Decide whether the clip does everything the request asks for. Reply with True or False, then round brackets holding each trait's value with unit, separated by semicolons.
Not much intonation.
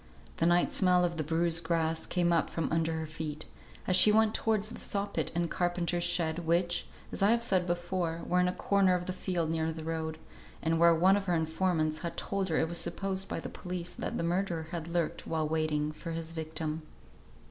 True (2.0 semitones)